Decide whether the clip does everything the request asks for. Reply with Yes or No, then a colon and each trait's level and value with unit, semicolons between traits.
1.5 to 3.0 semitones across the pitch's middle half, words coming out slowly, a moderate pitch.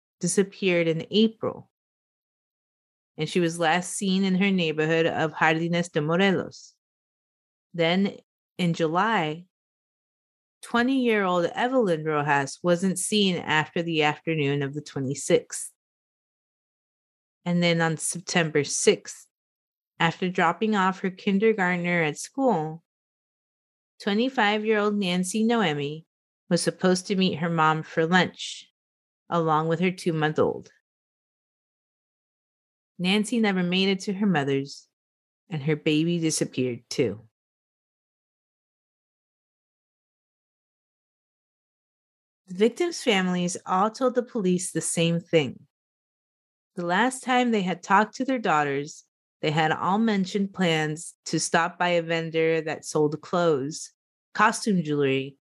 No: average, 4.0 semitones; slow, 115 wpm; medium, 175 Hz